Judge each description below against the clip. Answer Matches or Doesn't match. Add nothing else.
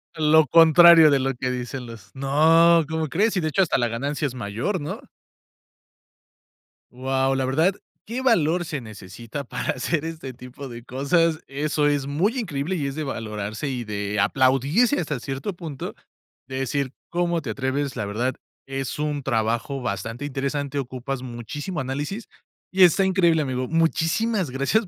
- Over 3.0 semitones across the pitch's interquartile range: Matches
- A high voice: Doesn't match